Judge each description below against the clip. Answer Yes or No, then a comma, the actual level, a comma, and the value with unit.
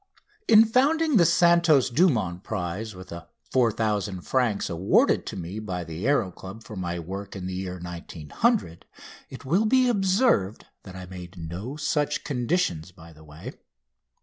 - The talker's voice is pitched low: Yes, low, 100 Hz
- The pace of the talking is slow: No, average, 155 wpm